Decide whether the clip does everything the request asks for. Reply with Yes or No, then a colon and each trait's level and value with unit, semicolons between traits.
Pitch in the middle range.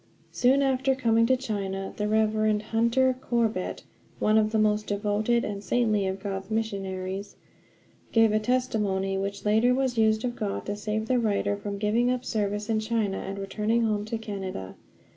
No: high, 215 Hz